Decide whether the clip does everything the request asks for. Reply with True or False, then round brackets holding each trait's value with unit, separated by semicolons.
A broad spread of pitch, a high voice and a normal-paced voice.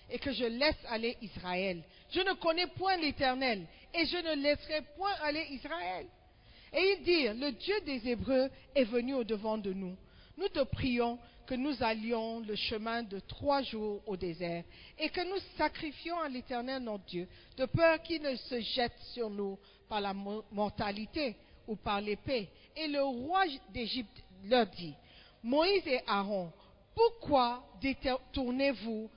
True (5.7 semitones; 250 Hz; 155 wpm)